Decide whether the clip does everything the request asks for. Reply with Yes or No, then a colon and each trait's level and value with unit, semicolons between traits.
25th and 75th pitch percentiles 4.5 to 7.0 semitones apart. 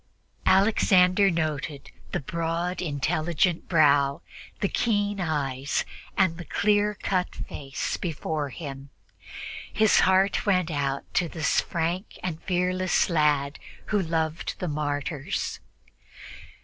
No: average, 4.1 semitones